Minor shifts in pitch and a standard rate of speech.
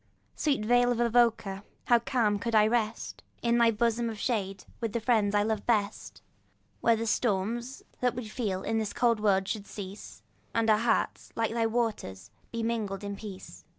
Yes: narrow, 2.3 semitones; average, 185 wpm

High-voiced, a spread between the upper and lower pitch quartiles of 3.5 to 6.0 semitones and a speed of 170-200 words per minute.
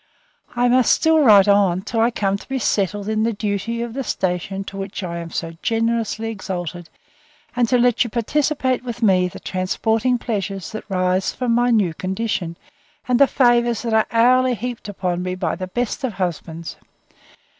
Yes: high, 220 Hz; average, 4.3 semitones; average, 185 wpm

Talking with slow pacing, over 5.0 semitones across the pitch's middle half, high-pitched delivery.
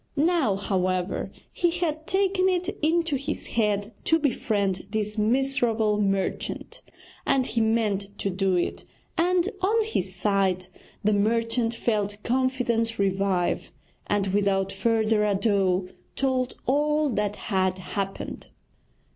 Yes: slow, 120 wpm; wide, 5.4 semitones; high, 215 Hz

